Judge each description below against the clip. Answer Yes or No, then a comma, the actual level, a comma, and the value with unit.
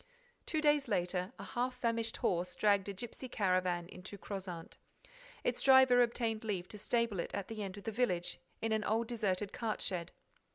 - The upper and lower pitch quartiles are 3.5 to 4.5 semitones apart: Yes, average, 4.1 semitones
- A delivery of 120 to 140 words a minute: No, average, 180 wpm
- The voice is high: Yes, high, 210 Hz